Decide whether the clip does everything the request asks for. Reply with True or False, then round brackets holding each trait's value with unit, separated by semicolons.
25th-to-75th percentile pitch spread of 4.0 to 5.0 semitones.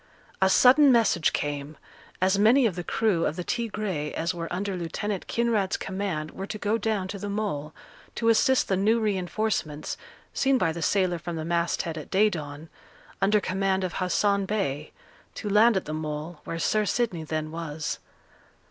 True (4.5 semitones)